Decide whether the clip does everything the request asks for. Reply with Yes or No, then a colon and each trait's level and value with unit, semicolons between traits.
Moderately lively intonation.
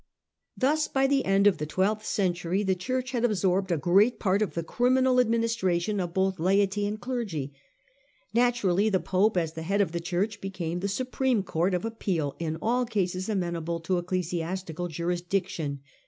Yes: average, 4.0 semitones